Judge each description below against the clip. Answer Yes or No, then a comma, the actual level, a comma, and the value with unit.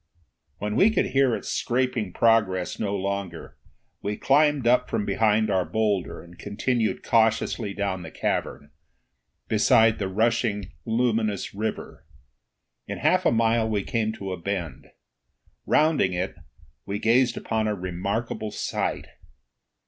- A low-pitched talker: Yes, low, 110 Hz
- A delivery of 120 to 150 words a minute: Yes, slow, 135 wpm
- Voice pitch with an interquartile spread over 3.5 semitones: No, average, 2.8 semitones